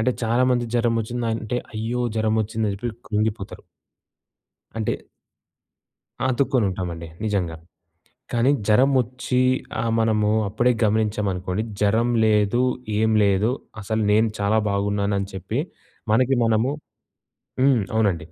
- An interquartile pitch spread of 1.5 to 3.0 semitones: Yes, narrow, 2.6 semitones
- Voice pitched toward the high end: No, low, 110 Hz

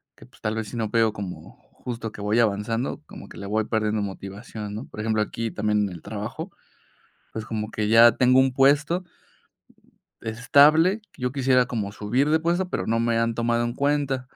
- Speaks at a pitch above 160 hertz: No, low, 115 Hz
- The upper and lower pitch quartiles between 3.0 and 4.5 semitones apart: Yes, average, 3.5 semitones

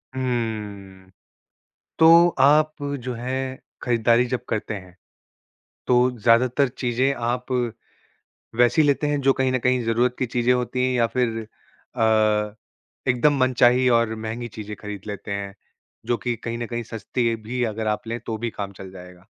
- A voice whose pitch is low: Yes, low, 120 Hz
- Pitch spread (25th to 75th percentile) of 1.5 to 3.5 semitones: Yes, average, 2.7 semitones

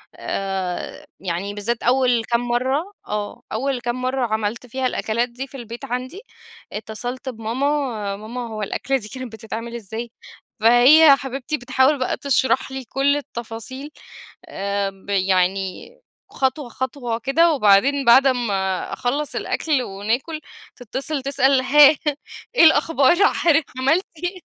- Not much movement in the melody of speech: No, average, 3.8 semitones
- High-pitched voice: Yes, very high, 250 Hz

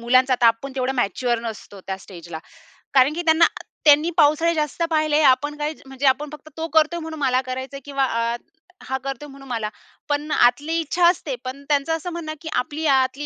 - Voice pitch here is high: Yes, very high, 280 Hz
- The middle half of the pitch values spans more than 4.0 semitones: No, average, 3.3 semitones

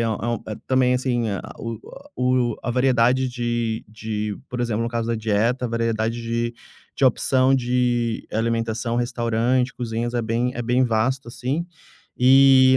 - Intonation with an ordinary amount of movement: No, narrow, 1.7 semitones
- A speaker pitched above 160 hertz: No, low, 120 Hz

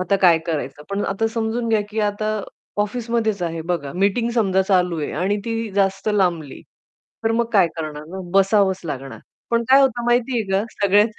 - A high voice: Yes, high, 200 Hz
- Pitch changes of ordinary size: Yes, average, 3.9 semitones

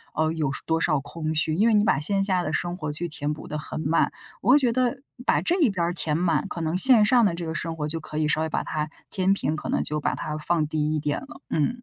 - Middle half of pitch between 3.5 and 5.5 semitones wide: Yes, average, 4.2 semitones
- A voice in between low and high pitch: Yes, medium, 165 Hz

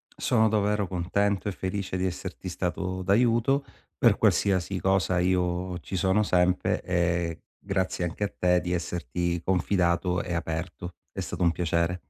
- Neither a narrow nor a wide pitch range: No, narrow, 1.8 semitones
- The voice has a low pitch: Yes, very low, 90 Hz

